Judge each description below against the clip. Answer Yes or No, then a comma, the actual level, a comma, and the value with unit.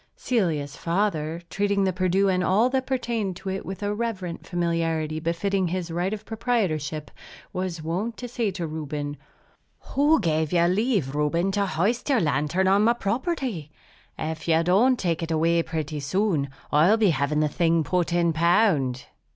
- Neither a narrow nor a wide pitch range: Yes, average, 4.4 semitones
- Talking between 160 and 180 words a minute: Yes, average, 165 wpm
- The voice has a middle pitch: Yes, medium, 175 Hz